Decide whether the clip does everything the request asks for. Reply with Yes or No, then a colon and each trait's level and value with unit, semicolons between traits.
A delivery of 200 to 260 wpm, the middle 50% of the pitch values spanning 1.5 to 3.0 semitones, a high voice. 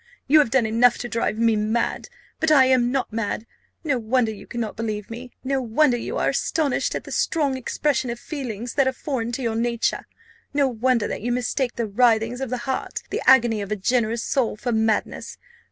Yes: fast, 205 wpm; average, 2.7 semitones; high, 240 Hz